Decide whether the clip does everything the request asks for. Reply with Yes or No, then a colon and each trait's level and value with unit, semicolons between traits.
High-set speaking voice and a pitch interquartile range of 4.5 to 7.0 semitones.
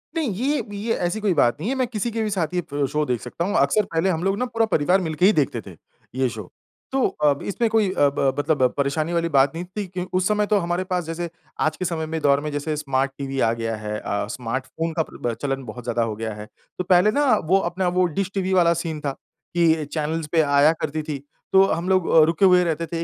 No: medium, 165 Hz; average, 5.0 semitones